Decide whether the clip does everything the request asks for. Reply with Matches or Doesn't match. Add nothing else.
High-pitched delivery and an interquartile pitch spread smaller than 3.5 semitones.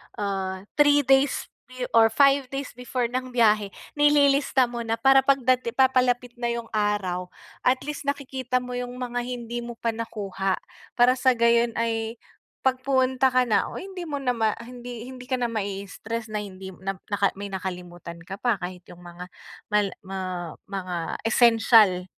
Doesn't match